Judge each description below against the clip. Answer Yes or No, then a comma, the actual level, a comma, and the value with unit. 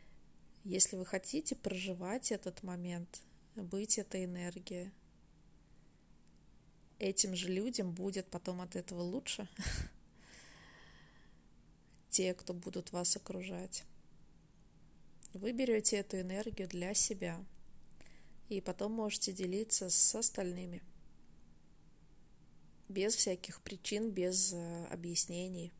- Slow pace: Yes, slow, 90 wpm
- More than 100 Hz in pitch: Yes, medium, 185 Hz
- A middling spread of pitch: No, narrow, 2.3 semitones